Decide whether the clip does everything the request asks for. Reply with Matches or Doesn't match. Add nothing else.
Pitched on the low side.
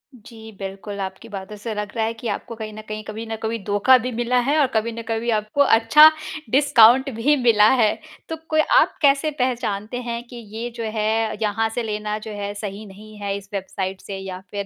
Doesn't match